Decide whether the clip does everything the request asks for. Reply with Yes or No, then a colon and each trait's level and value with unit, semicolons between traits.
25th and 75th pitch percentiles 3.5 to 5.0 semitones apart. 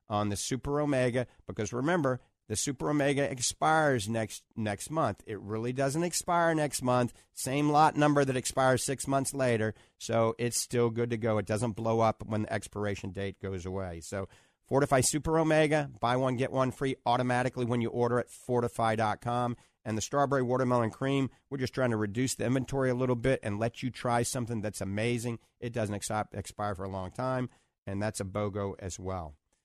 Yes: average, 3.8 semitones